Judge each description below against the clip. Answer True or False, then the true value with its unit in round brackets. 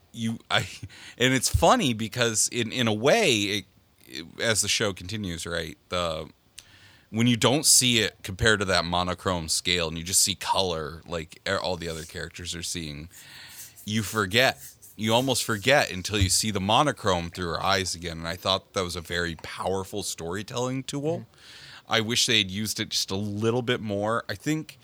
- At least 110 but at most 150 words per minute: False (185 wpm)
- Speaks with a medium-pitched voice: False (105 Hz)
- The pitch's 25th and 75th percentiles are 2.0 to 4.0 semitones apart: False (4.6 semitones)